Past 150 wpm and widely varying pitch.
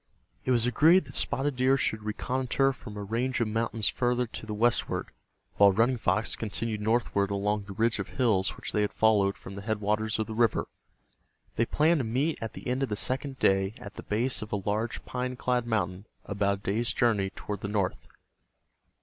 No: average, 200 wpm; average, 3.3 semitones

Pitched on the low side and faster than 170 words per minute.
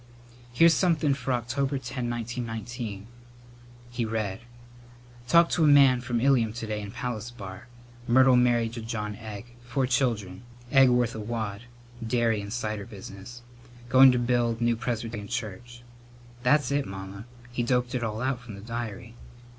No: low, 120 Hz; average, 155 wpm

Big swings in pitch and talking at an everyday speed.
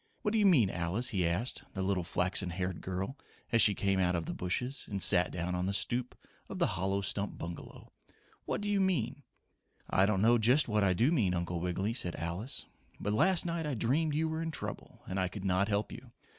No: wide, 5.8 semitones; fast, 225 wpm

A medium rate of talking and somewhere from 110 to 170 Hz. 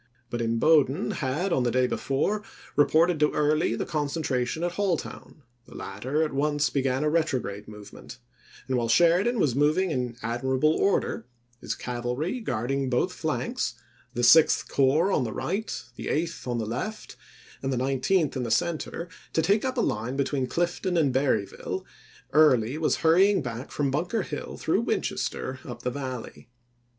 Yes: average, 165 wpm; medium, 140 Hz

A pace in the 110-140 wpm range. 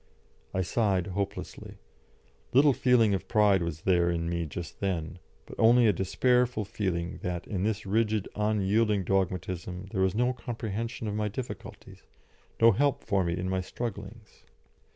No: average, 150 wpm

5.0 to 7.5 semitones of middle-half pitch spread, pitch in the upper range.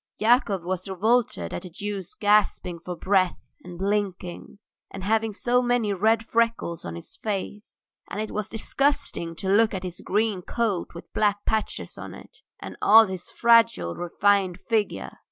No: average, 3.5 semitones; high, 205 Hz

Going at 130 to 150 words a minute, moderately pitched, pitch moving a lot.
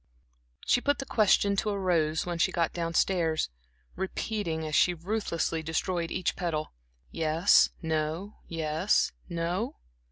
No: slow, 135 wpm; medium, 170 Hz; average, 3.4 semitones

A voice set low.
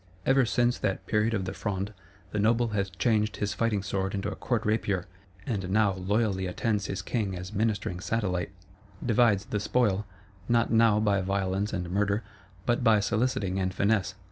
Yes: low, 105 Hz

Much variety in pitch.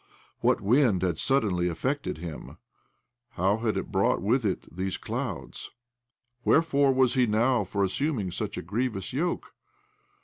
Yes: wide, 5.8 semitones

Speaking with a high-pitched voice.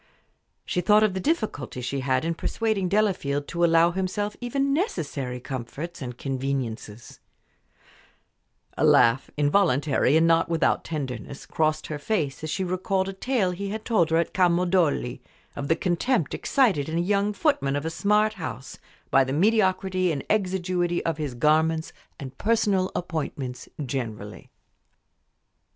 No: medium, 165 Hz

